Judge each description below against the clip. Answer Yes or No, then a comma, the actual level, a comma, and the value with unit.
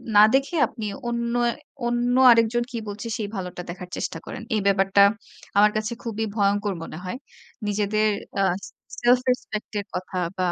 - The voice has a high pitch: Yes, high, 215 Hz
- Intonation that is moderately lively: Yes, average, 3.0 semitones